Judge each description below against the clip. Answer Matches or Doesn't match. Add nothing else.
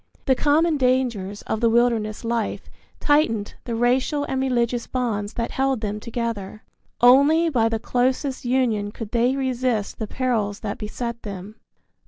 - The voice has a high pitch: Matches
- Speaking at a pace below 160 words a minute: Matches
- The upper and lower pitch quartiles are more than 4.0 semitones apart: Doesn't match